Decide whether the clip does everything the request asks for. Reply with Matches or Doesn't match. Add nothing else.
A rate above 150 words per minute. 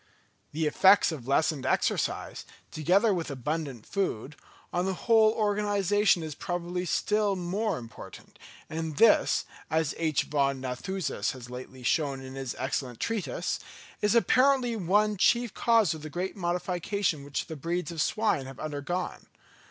Doesn't match